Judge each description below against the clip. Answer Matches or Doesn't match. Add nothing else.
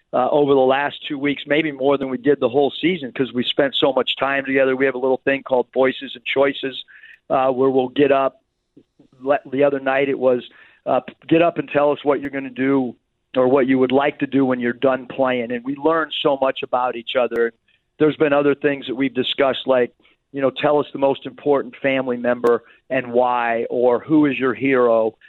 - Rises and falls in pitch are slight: Matches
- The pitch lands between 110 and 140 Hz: Matches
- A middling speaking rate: Doesn't match